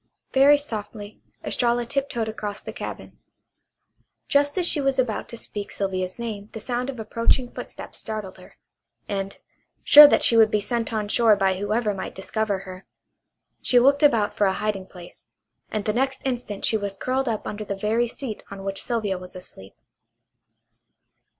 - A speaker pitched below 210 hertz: No, high, 215 Hz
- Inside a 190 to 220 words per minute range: No, average, 170 wpm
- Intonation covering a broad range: No, average, 3.4 semitones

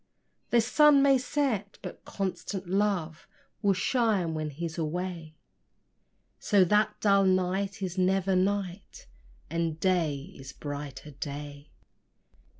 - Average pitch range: Yes, average, 4.2 semitones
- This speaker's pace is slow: Yes, slow, 115 wpm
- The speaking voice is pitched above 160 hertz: Yes, medium, 185 Hz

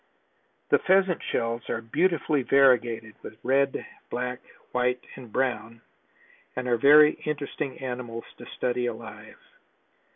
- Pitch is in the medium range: No, low, 125 Hz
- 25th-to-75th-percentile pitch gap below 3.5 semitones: Yes, average, 2.9 semitones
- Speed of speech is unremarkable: No, slow, 120 wpm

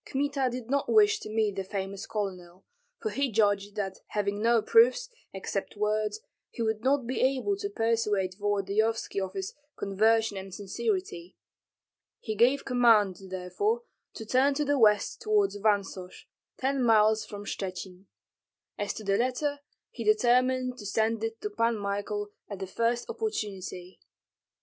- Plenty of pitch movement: No, average, 4.3 semitones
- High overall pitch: Yes, high, 220 Hz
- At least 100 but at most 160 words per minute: Yes, average, 150 wpm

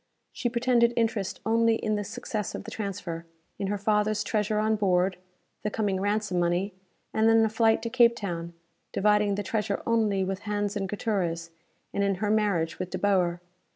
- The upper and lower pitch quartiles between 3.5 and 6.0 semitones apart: No, narrow, 2.4 semitones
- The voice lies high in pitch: Yes, high, 205 Hz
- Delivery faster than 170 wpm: Yes, average, 185 wpm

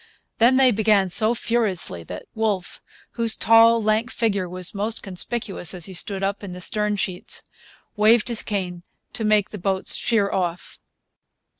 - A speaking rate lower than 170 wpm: Yes, average, 160 wpm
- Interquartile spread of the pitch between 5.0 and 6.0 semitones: No, average, 3.3 semitones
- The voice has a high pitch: Yes, high, 210 Hz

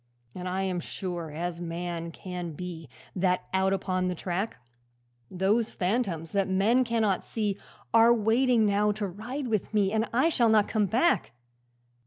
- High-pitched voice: Yes, high, 195 Hz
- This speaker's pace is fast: No, average, 160 wpm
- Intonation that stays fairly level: No, average, 3.8 semitones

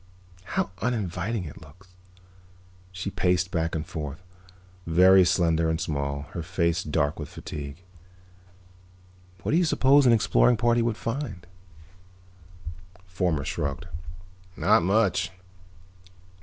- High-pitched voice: No, very low, 90 Hz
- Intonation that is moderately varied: Yes, average, 4.4 semitones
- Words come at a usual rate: No, slow, 115 wpm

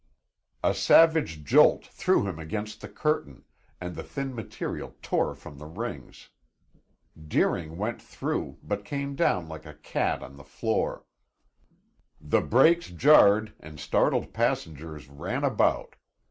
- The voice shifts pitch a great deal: Yes, wide, 7.7 semitones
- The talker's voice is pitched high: No, very low, 95 Hz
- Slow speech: Yes, slow, 130 wpm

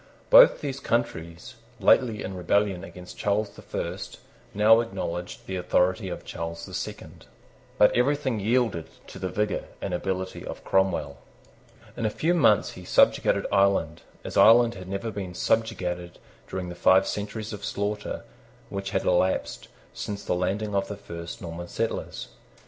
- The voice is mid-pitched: No, low, 100 Hz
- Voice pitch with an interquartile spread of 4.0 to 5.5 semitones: No, average, 3.3 semitones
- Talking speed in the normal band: Yes, average, 155 wpm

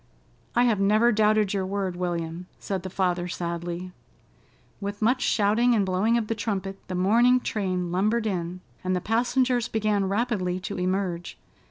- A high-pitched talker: Yes, high, 195 Hz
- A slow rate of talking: No, average, 160 wpm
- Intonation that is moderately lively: Yes, average, 3.4 semitones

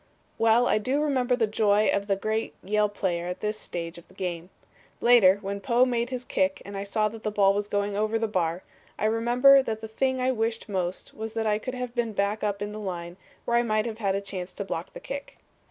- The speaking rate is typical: No, fast, 240 wpm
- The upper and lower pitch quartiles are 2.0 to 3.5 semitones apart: Yes, average, 2.9 semitones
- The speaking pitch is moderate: No, high, 215 Hz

